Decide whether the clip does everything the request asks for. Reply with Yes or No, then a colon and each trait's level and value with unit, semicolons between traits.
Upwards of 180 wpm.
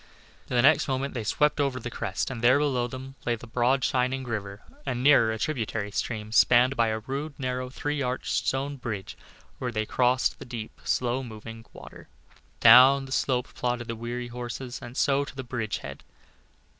Yes: average, 190 wpm